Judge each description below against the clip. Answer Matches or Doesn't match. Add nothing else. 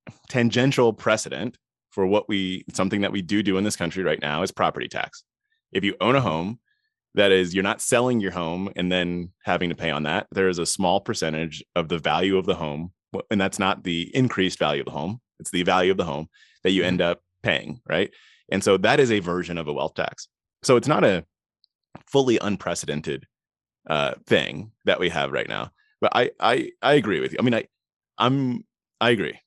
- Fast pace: Matches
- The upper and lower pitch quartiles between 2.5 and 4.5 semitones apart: Doesn't match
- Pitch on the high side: Doesn't match